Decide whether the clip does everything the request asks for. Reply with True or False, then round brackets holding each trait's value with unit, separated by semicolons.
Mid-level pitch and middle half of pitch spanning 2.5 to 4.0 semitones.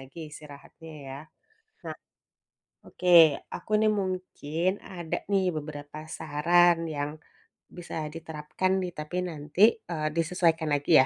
True (160 Hz; 2.8 semitones)